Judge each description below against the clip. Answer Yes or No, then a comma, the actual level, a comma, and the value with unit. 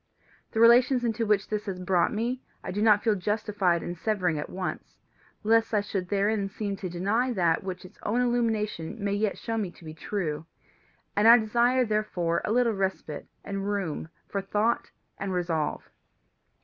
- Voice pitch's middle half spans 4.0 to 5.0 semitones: No, average, 3.5 semitones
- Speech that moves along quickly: No, average, 175 wpm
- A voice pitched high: Yes, high, 205 Hz